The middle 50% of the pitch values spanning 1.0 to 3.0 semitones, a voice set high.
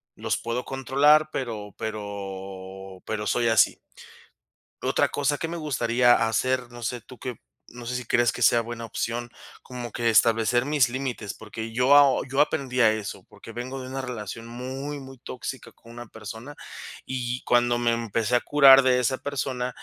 No: narrow, 2.5 semitones; low, 120 Hz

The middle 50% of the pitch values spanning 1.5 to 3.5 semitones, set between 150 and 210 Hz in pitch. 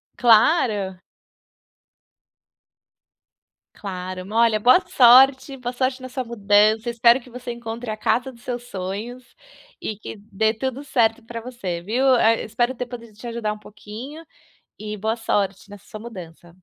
No: average, 2.8 semitones; high, 230 Hz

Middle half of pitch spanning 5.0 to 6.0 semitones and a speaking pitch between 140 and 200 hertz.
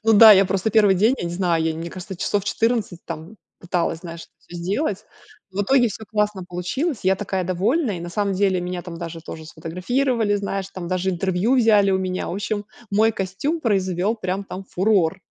No: average, 3.1 semitones; high, 190 Hz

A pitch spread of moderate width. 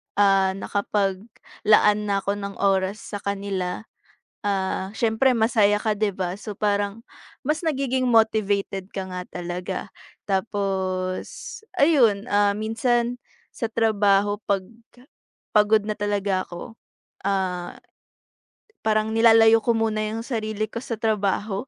No: narrow, 2.3 semitones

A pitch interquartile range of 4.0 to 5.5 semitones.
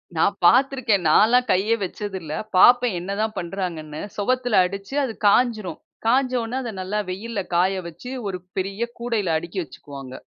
Yes: average, 4.7 semitones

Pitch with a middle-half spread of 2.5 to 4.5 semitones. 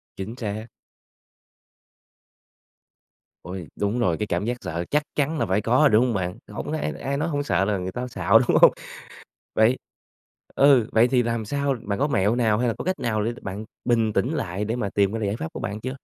Yes: average, 3.9 semitones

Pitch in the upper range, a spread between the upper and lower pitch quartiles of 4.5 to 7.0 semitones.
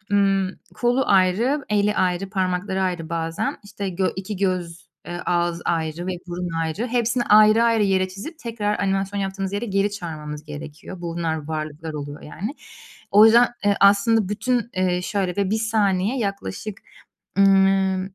No: high, 195 Hz; average, 3.2 semitones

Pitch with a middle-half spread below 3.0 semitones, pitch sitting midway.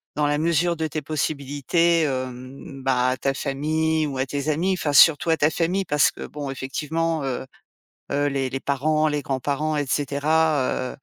Yes: narrow, 2.6 semitones; medium, 145 Hz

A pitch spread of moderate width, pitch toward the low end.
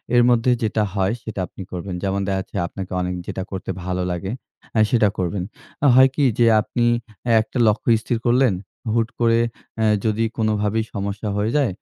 Yes: average, 3.1 semitones; low, 105 Hz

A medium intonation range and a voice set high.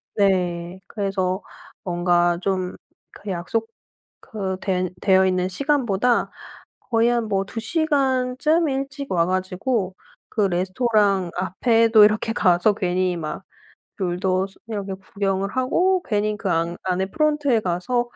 Yes: average, 4.4 semitones; high, 195 Hz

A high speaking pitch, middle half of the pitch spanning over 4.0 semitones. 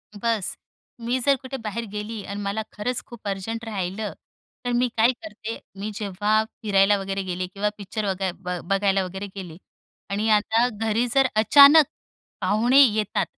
No: high, 210 Hz; average, 2.8 semitones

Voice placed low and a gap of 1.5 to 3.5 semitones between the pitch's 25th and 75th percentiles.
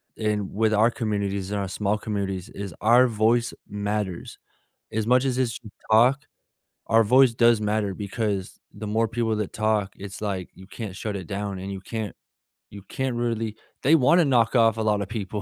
Yes: low, 110 Hz; narrow, 2.5 semitones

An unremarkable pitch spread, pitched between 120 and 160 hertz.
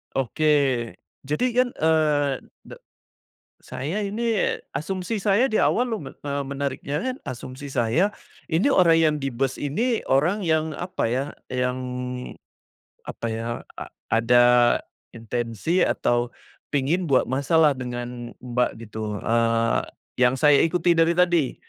No: wide, 5.7 semitones; medium, 140 Hz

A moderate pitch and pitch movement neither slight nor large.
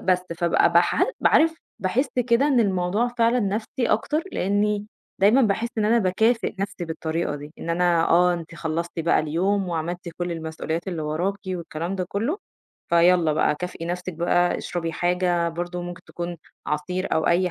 Yes: medium, 180 Hz; average, 3.2 semitones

